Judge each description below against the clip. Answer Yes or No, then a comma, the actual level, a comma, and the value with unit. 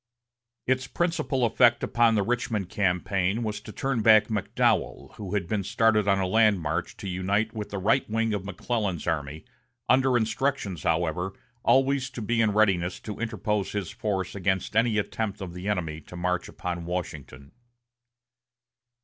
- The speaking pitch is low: Yes, low, 105 Hz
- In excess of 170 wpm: No, average, 160 wpm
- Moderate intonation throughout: Yes, average, 3.9 semitones